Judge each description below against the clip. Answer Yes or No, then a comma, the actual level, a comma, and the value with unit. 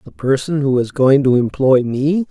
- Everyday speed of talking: No, fast, 210 wpm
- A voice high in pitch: No, low, 135 Hz